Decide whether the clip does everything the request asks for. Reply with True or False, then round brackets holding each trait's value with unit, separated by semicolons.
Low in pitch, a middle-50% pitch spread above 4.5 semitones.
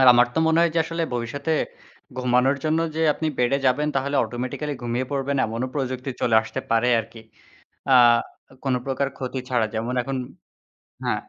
False (130 Hz; 2.6 semitones)